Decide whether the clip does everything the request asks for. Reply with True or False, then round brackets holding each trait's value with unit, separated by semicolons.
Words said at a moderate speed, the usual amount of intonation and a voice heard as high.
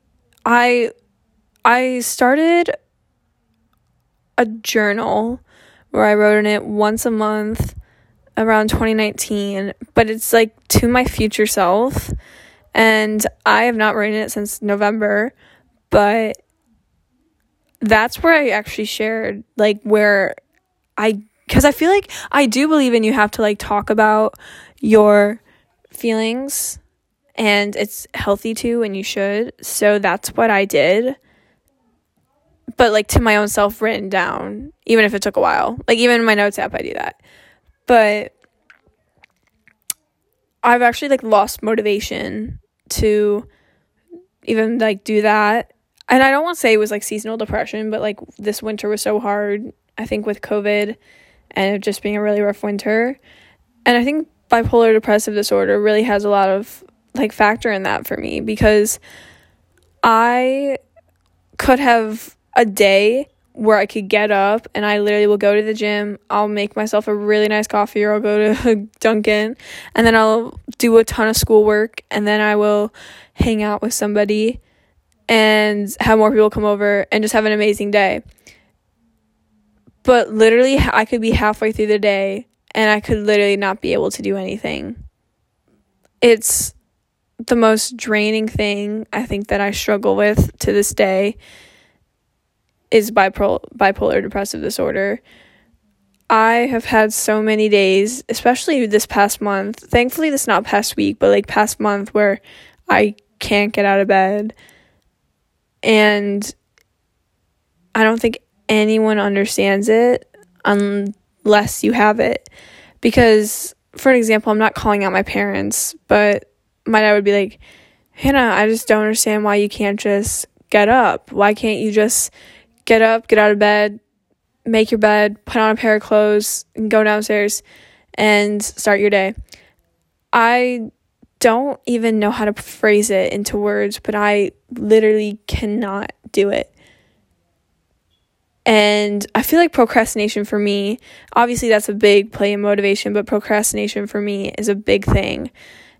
False (155 wpm; 1.7 semitones; 210 Hz)